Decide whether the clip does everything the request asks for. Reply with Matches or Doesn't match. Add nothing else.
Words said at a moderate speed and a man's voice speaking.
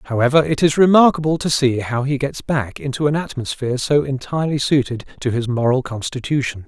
Matches